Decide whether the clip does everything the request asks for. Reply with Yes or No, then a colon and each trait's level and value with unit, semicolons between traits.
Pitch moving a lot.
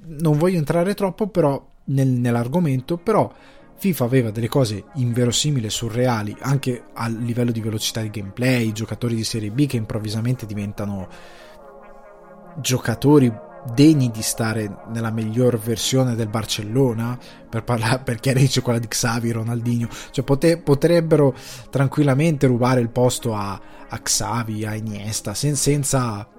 No: average, 3.6 semitones